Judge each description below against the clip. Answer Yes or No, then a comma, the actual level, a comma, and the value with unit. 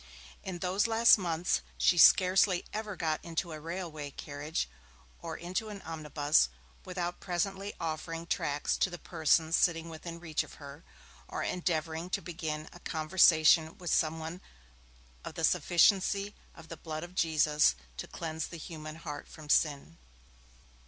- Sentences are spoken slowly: No, average, 150 wpm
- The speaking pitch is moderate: Yes, medium, 165 Hz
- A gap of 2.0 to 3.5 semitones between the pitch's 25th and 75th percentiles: Yes, narrow, 2.4 semitones